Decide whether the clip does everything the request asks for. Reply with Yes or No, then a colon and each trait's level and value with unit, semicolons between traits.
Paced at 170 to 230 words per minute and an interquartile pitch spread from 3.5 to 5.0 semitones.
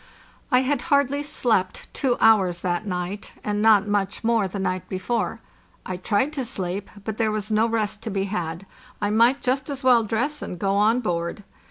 Yes: average, 190 wpm; average, 4.1 semitones